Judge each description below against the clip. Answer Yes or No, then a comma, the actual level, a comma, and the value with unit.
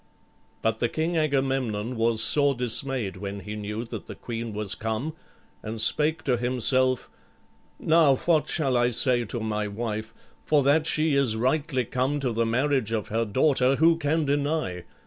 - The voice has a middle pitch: No, low, 125 Hz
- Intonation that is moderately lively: Yes, average, 4.4 semitones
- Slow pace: No, average, 165 wpm